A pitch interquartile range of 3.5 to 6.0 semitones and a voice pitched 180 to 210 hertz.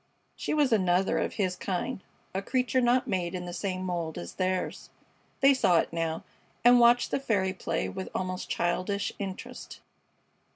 Yes: average, 4.9 semitones; high, 190 Hz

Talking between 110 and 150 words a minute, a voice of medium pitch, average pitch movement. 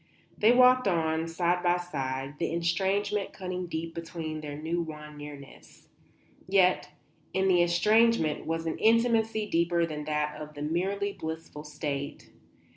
Yes: average, 140 wpm; medium, 170 Hz; average, 3.9 semitones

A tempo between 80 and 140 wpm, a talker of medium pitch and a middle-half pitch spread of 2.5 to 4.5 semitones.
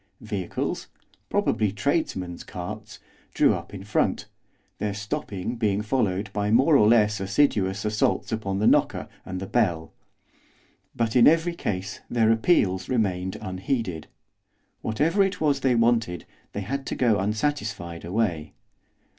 No: slow, 135 wpm; low, 105 Hz; average, 4.1 semitones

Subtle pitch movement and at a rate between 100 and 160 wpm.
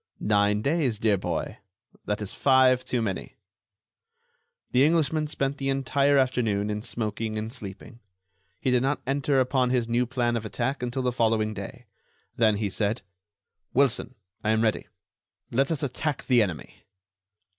No: average, 3.9 semitones; average, 155 wpm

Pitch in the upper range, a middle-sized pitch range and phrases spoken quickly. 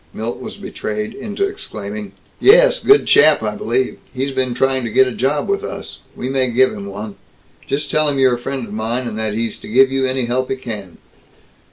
No: low, 130 Hz; average, 3.6 semitones; fast, 215 wpm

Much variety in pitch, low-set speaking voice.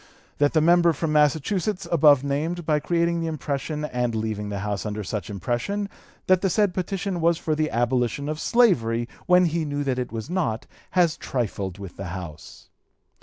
No: wide, 6.8 semitones; medium, 150 Hz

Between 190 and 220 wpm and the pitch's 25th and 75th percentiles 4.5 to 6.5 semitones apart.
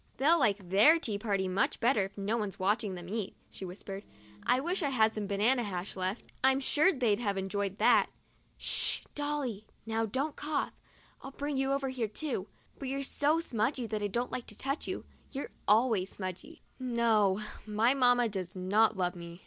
Yes: average, 195 wpm; average, 5.2 semitones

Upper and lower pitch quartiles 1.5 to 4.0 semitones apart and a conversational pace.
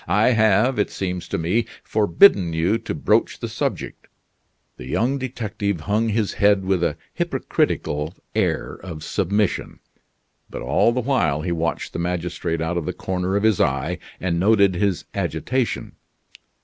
No: average, 4.5 semitones; average, 155 wpm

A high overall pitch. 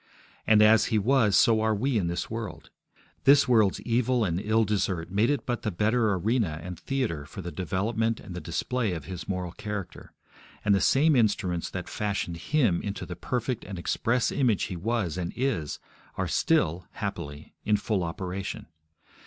No: low, 105 Hz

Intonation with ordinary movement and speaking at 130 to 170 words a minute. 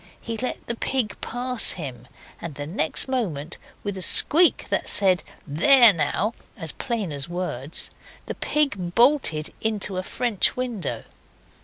No: wide, 7.3 semitones; average, 145 wpm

